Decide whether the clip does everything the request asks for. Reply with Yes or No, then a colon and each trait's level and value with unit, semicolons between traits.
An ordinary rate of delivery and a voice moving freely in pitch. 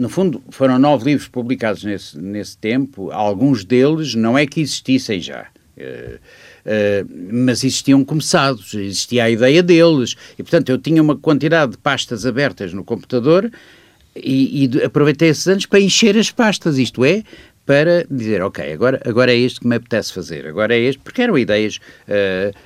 Yes: average, 170 wpm; wide, 5.8 semitones